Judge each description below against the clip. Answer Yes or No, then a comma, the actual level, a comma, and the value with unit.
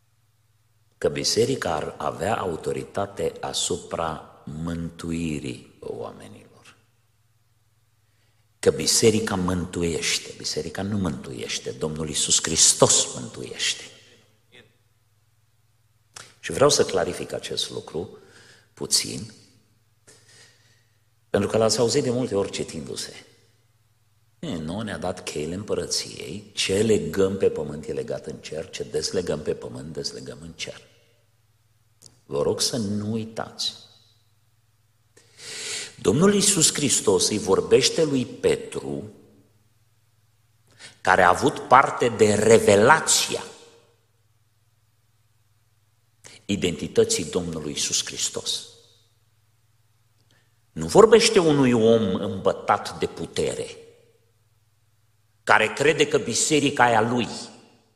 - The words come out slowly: Yes, slow, 90 wpm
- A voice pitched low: Yes, low, 115 Hz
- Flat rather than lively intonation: Yes, narrow, 1.8 semitones